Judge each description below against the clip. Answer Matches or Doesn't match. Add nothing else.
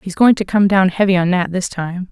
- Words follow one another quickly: Matches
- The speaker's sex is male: Doesn't match